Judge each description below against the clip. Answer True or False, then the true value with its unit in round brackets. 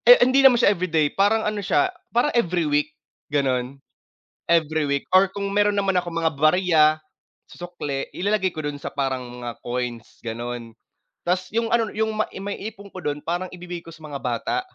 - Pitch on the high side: False (175 Hz)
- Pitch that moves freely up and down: True (5.7 semitones)